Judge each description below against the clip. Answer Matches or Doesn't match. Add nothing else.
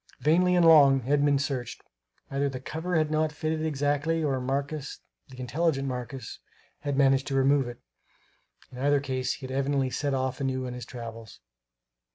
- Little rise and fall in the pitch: Matches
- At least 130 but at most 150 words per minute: Doesn't match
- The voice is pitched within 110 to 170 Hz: Matches